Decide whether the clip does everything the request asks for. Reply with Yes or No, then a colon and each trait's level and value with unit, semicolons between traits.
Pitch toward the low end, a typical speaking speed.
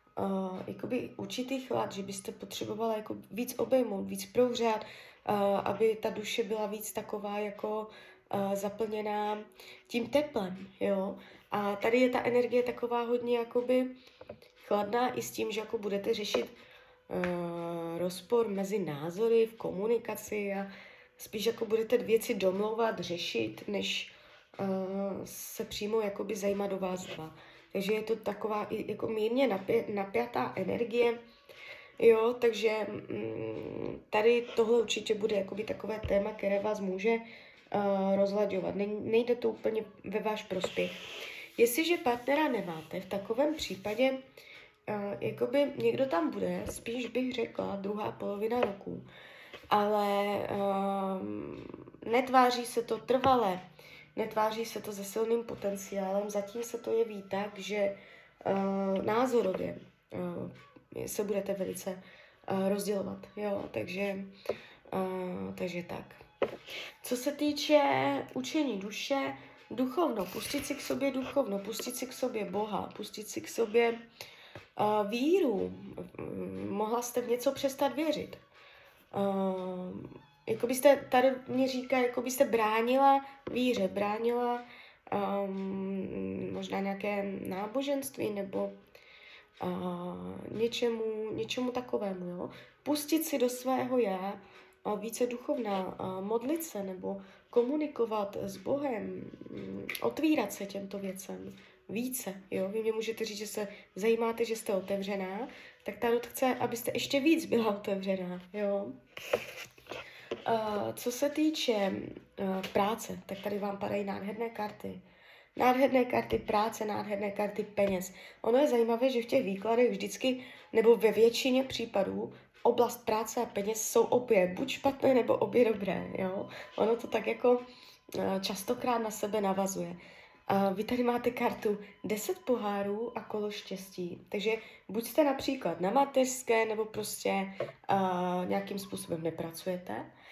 No: high, 215 Hz; average, 130 wpm